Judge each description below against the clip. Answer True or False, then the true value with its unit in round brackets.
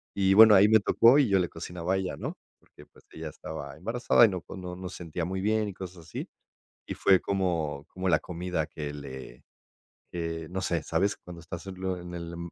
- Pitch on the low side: True (90 Hz)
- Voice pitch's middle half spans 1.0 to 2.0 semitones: False (2.7 semitones)